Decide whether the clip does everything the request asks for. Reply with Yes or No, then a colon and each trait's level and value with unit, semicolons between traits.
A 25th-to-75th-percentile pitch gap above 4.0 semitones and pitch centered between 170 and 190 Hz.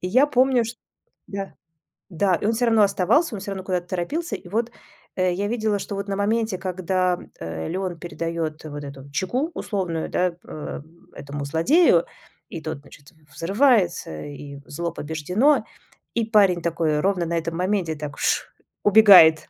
Yes: average, 4.6 semitones; medium, 185 Hz